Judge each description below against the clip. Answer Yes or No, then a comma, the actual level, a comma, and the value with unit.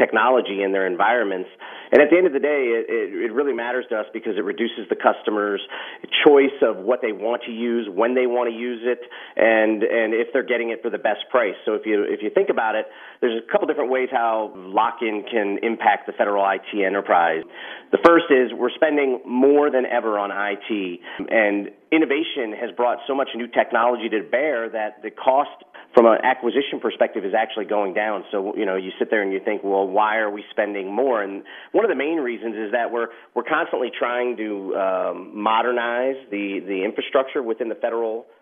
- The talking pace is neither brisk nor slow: No, fast, 210 wpm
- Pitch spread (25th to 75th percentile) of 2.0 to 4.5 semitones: Yes, average, 3.9 semitones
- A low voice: Yes, low, 115 Hz